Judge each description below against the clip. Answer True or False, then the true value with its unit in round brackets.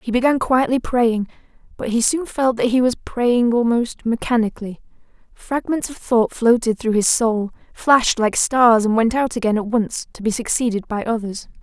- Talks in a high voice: True (235 Hz)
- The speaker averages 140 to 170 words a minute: False (180 wpm)